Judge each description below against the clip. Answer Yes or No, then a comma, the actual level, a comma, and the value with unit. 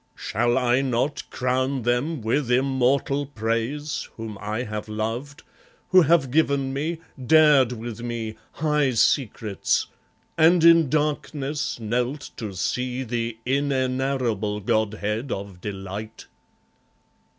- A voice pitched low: Yes, low, 125 Hz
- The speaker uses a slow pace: Yes, slow, 110 wpm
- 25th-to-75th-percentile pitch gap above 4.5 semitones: No, average, 4.1 semitones